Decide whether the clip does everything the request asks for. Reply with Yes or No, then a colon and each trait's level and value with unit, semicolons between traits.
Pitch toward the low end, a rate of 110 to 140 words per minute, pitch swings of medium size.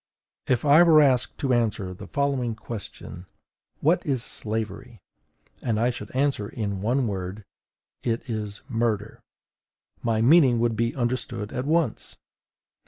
Yes: low, 120 Hz; slow, 135 wpm; average, 4.0 semitones